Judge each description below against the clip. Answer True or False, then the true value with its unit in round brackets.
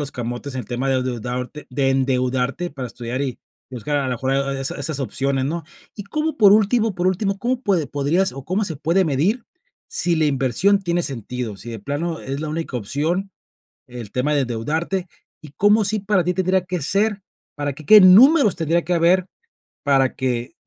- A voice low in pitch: False (150 Hz)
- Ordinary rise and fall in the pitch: False (6.2 semitones)